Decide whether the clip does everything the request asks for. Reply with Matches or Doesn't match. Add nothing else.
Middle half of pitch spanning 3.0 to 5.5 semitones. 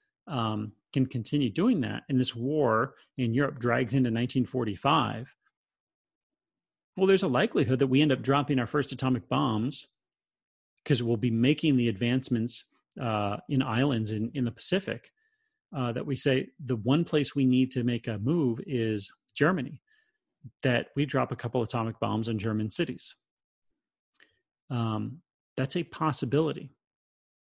Matches